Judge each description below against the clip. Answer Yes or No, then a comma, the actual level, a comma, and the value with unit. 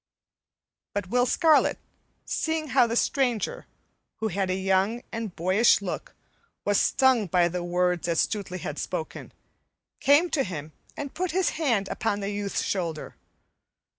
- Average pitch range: No, wide, 6.3 semitones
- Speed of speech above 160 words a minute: No, average, 145 wpm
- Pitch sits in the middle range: No, high, 205 Hz